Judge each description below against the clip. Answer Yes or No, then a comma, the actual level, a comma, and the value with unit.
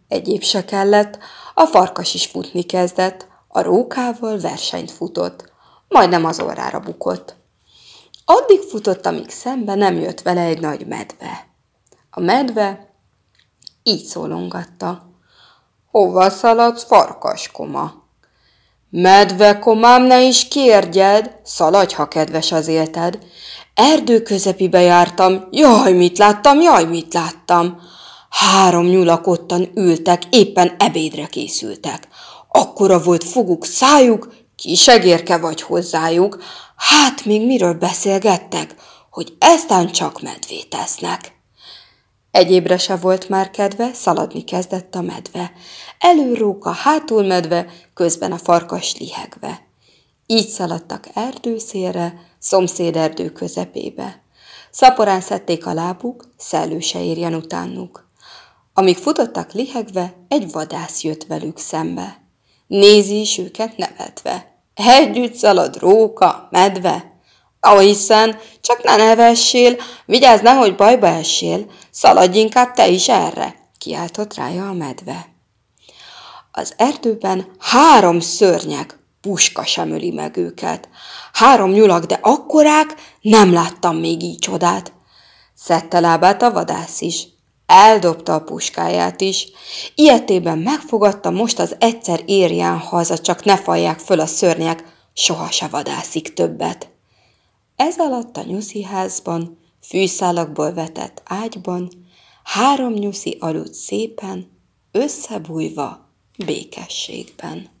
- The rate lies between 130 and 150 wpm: No, average, 110 wpm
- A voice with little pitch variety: No, average, 4.5 semitones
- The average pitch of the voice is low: No, high, 190 Hz